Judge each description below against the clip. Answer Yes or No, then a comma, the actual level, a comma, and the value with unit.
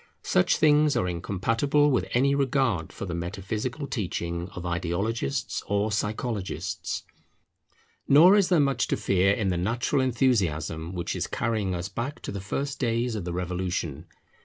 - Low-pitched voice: Yes, low, 100 Hz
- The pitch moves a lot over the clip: Yes, wide, 6.6 semitones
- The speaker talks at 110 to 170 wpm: Yes, average, 155 wpm